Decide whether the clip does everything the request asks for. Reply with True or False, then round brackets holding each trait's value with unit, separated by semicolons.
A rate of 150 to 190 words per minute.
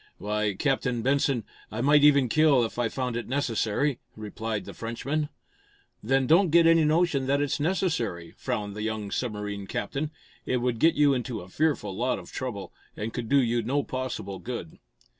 True (180 wpm)